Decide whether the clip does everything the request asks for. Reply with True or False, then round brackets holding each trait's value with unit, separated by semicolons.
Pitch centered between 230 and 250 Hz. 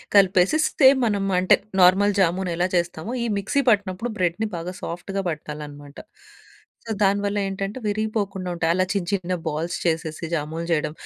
False (185 Hz)